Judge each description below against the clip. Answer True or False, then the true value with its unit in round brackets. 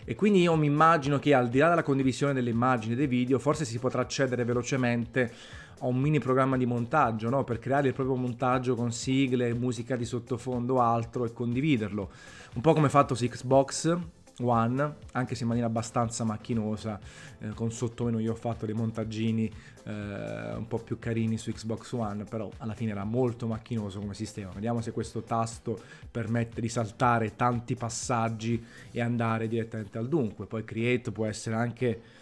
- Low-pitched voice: True (120 Hz)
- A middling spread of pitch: False (2.2 semitones)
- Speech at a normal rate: False (185 wpm)